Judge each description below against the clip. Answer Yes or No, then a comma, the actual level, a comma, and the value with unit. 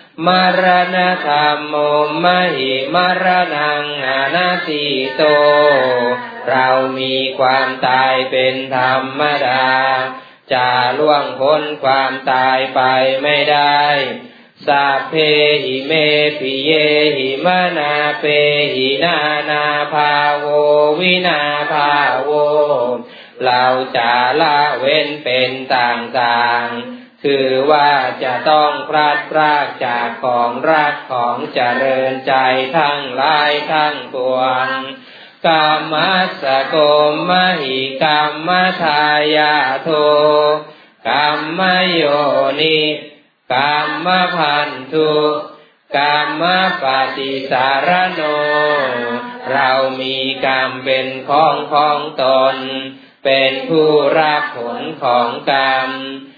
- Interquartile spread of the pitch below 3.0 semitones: Yes, narrow, 2.4 semitones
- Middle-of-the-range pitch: Yes, medium, 145 Hz